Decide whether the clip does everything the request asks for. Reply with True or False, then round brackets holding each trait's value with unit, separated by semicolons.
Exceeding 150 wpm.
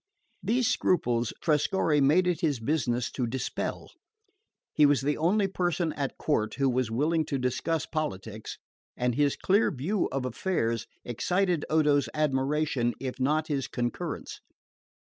False (140 wpm)